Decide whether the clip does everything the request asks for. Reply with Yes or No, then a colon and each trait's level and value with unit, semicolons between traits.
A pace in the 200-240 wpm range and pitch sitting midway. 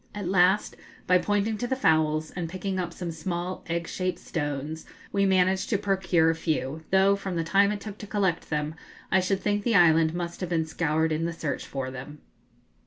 Yes: fast, 205 wpm; medium, 175 Hz